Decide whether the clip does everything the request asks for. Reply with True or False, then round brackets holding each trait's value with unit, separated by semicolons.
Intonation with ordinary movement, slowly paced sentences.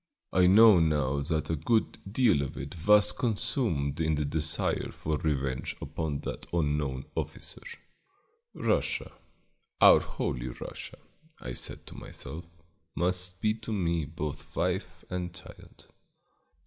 True (4.2 semitones; 130 wpm)